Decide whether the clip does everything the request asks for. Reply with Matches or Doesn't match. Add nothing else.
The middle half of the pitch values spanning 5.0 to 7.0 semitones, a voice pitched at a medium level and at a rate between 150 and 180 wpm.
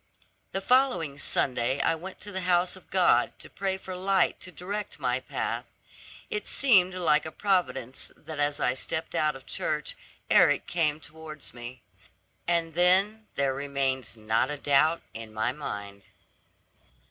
Matches